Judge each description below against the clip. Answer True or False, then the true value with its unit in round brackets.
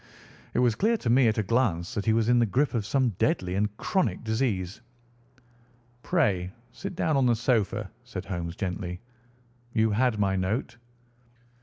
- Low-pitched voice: True (110 Hz)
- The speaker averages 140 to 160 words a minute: False (170 wpm)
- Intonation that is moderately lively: True (4.6 semitones)